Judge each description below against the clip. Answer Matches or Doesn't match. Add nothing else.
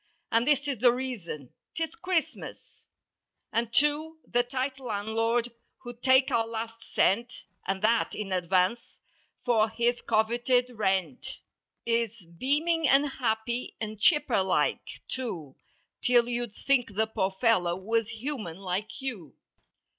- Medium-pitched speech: Doesn't match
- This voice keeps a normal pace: Doesn't match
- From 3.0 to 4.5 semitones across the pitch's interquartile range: Matches